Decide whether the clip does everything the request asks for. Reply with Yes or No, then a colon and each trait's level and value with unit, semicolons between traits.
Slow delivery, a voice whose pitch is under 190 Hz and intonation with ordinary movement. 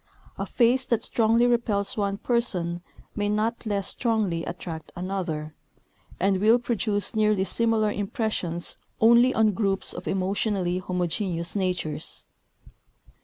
No: slow, 120 wpm; high, 205 Hz; average, 3.7 semitones